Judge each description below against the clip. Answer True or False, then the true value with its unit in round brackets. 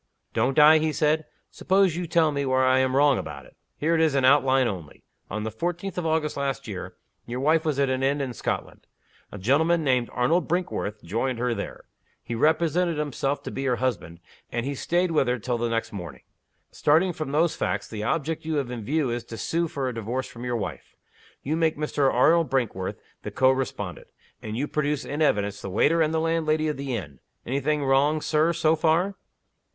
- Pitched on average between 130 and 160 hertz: True (140 Hz)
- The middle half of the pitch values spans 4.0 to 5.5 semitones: True (4.7 semitones)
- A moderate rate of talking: False (210 wpm)